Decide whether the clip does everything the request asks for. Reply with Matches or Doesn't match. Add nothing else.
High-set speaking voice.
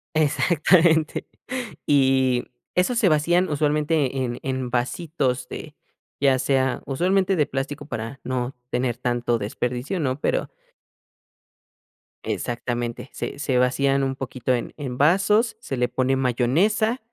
Doesn't match